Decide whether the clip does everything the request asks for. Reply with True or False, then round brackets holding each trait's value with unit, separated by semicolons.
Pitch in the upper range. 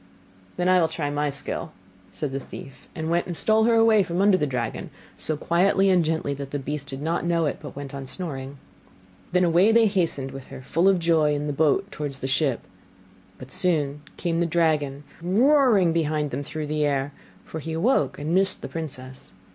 False (160 Hz)